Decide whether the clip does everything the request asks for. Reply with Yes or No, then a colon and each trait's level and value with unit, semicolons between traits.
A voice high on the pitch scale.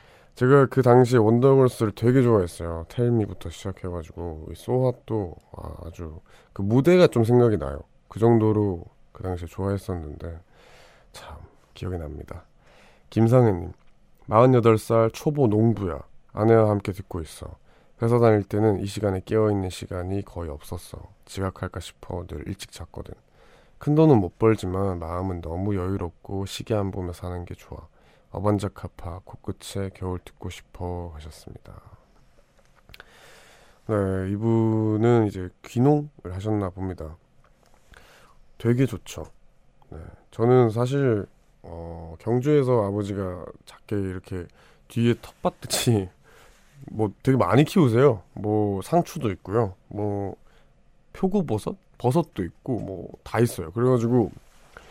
No: low, 100 Hz